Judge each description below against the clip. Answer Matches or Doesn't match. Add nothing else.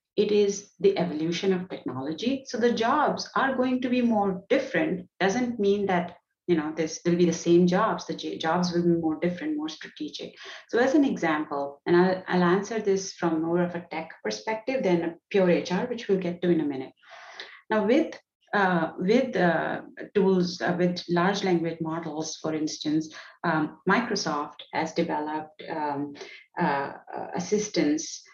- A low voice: Doesn't match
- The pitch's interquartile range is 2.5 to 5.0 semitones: Matches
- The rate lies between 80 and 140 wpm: Doesn't match